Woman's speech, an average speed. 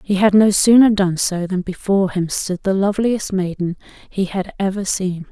Yes: female; average, 190 wpm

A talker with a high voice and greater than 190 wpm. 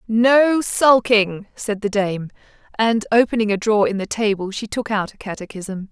No: high, 215 Hz; average, 175 wpm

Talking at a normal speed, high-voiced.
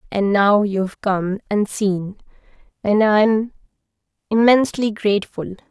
No: slow, 95 wpm; high, 205 Hz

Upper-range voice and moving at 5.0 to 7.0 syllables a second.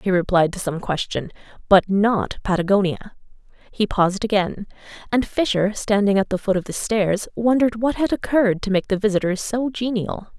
Yes: high, 205 Hz; 5.2 syllables/s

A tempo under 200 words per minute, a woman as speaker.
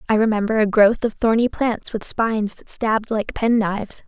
No: fast, 205 wpm; female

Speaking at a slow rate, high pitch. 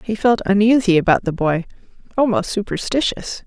Yes: slow, 120 wpm; high, 200 Hz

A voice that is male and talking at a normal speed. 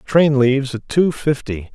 Yes: male; average, 170 wpm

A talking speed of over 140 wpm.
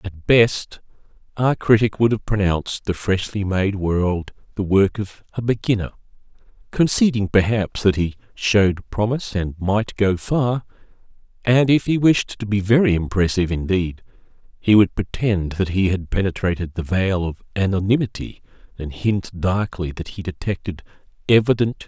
Yes: average, 160 wpm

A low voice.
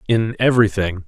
Yes: low, 105 Hz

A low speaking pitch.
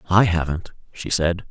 Yes: very low, 85 Hz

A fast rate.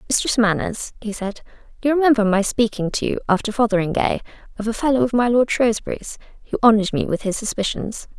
No: average, 185 wpm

